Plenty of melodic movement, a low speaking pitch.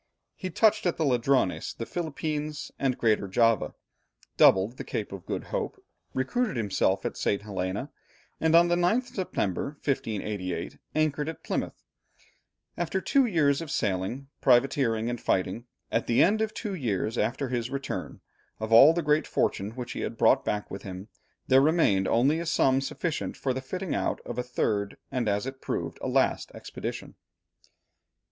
Yes: wide, 6.4 semitones; low, 130 Hz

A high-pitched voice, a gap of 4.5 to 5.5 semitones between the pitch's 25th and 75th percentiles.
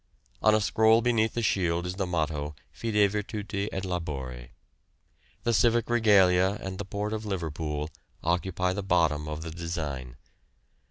No: very low, 95 Hz; average, 4.8 semitones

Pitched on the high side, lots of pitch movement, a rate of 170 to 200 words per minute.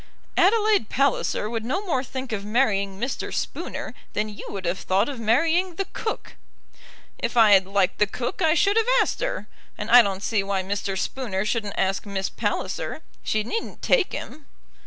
Yes: high, 225 Hz; wide, 7.6 semitones; average, 180 wpm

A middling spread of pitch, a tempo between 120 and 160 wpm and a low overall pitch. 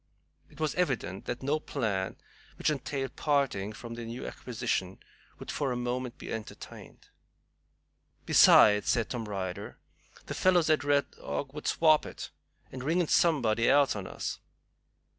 Yes: average, 5.0 semitones; average, 150 wpm; low, 125 Hz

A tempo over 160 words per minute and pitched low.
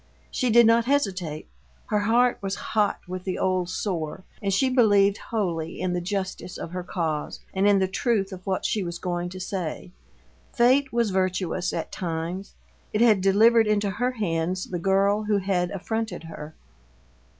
No: average, 170 wpm; high, 195 Hz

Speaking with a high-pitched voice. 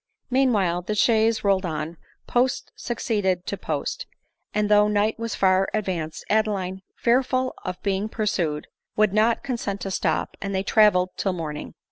Yes: high, 205 Hz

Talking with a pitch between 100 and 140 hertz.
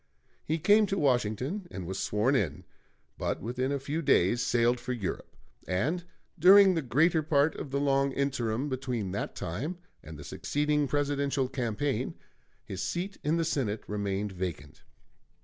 Yes: low, 135 Hz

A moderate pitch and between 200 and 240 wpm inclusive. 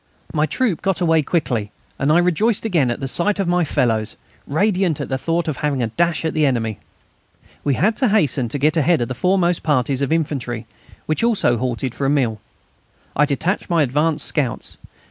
Yes: medium, 150 Hz; fast, 205 wpm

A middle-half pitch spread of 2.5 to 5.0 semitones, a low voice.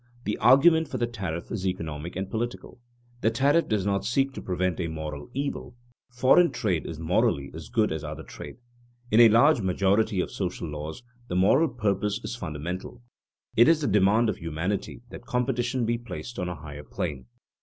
No: wide, 5.5 semitones; low, 105 Hz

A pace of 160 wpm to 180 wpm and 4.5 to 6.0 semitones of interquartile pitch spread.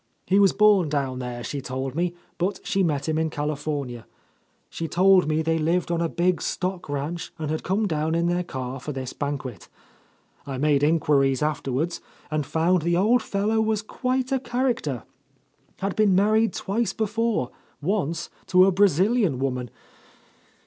Yes: average, 165 wpm; wide, 5.5 semitones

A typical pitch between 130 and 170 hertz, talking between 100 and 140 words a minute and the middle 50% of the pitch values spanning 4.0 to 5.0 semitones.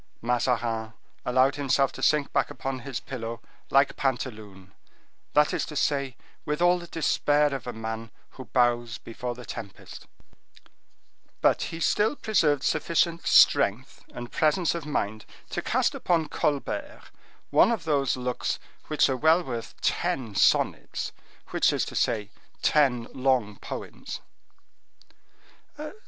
Yes: low, 135 Hz; slow, 135 wpm; average, 4.3 semitones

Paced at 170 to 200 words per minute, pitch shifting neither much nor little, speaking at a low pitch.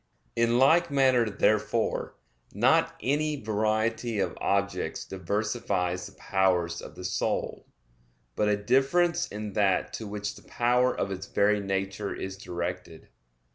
No: slow, 135 wpm; average, 4.2 semitones; low, 105 Hz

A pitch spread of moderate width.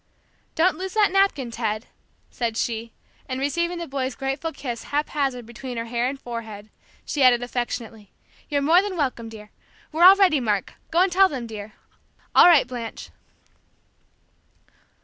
No: wide, 5.8 semitones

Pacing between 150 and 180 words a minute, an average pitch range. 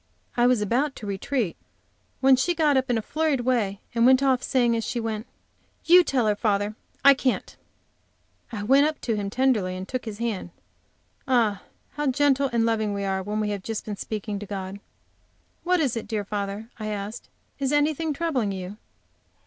No: average, 190 wpm; average, 4.5 semitones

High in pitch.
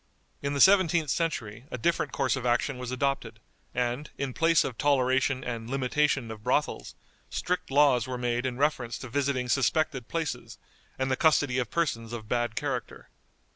No: low, 130 Hz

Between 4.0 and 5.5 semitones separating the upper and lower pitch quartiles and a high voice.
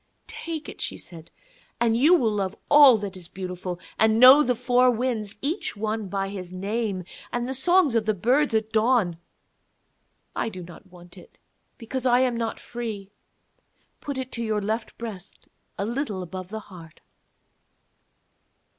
Yes: average, 4.5 semitones; high, 220 Hz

